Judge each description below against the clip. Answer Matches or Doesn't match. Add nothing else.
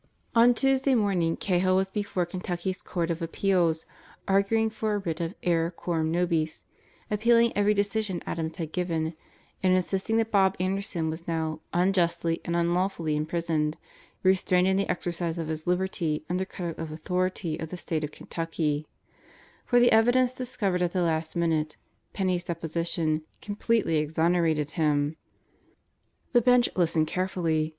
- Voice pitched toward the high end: Doesn't match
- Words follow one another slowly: Doesn't match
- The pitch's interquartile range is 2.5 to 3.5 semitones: Matches